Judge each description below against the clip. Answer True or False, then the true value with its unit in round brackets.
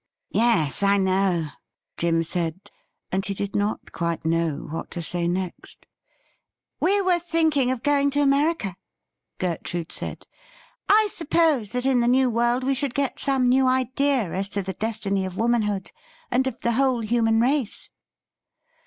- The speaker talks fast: False (160 wpm)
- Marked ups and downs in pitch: True (6.1 semitones)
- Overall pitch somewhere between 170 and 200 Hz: False (230 Hz)